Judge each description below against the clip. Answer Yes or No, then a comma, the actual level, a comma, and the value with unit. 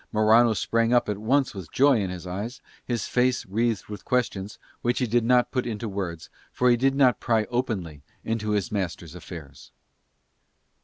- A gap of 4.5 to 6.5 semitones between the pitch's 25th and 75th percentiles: No, average, 4.0 semitones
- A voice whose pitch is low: Yes, low, 110 Hz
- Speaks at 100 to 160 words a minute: No, average, 175 wpm